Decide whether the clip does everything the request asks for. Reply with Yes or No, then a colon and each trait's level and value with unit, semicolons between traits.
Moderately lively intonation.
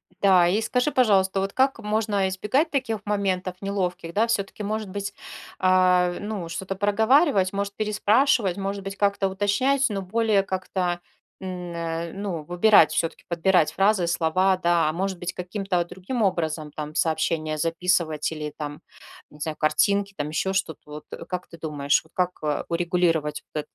Yes: average, 3.3 semitones